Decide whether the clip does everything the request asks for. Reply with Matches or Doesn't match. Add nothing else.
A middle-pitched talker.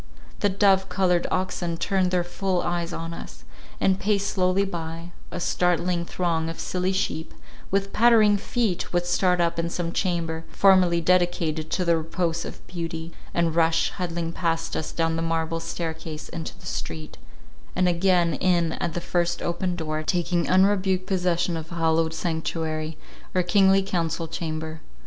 Matches